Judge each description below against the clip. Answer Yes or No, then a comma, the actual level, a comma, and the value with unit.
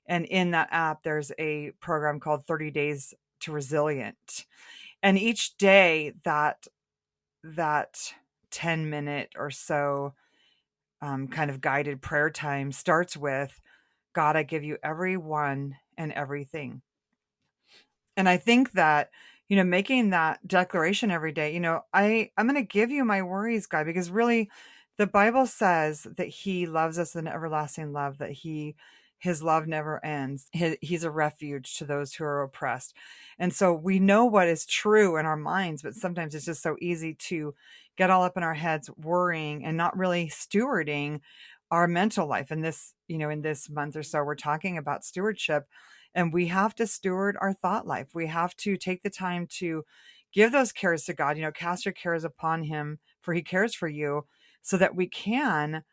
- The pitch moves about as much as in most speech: Yes, average, 3.8 semitones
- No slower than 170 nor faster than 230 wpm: Yes, average, 175 wpm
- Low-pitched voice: No, medium, 165 Hz